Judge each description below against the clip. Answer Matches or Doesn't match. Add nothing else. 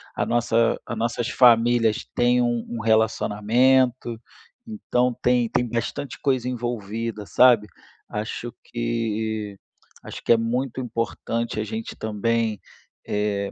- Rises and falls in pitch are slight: Matches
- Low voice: Matches